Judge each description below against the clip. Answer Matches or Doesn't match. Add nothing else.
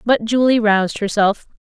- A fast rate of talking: Doesn't match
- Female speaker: Matches